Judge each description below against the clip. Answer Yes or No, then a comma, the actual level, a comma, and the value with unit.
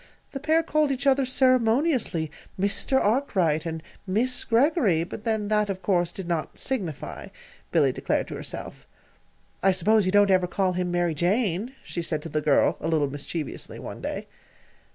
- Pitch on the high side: Yes, high, 195 Hz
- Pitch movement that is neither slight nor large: No, wide, 6.9 semitones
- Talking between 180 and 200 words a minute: No, average, 170 wpm